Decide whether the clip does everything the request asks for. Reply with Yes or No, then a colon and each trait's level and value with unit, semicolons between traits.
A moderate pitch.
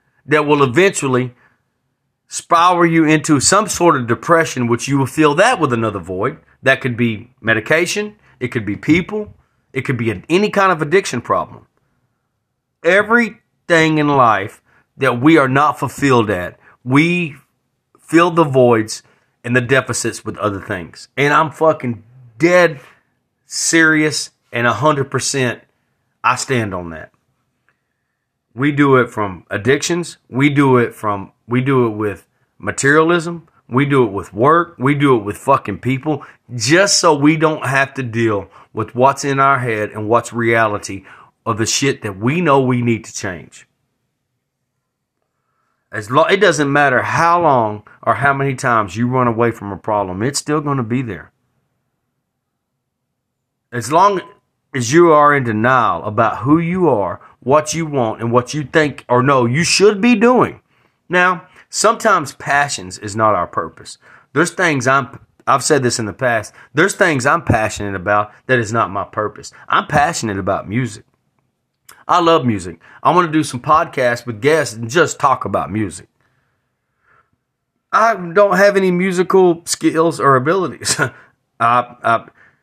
No: low, 130 Hz